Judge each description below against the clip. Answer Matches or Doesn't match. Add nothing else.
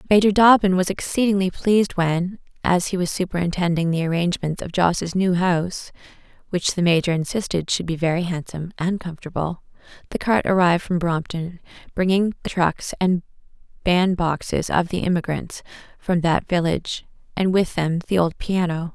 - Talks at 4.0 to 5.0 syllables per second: Doesn't match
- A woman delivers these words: Matches